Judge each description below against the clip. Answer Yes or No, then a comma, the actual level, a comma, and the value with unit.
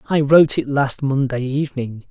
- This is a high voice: No, low, 135 Hz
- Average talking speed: Yes, average, 170 wpm